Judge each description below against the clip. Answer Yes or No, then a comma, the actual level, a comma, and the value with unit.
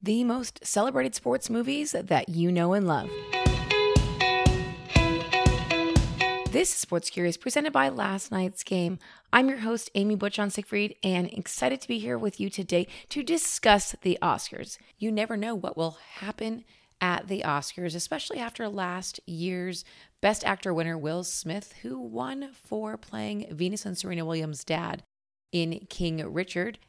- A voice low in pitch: No, medium, 180 Hz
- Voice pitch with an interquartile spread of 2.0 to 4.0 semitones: No, average, 4.5 semitones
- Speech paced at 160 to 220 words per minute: No, average, 150 wpm